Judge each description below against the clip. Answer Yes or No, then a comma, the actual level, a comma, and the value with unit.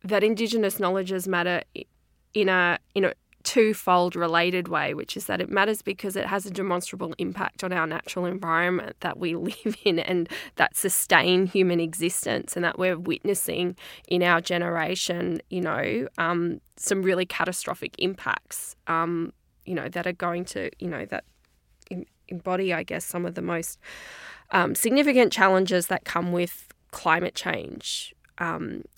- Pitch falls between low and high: Yes, medium, 180 Hz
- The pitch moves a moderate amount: No, narrow, 2.0 semitones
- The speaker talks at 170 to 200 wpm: No, average, 155 wpm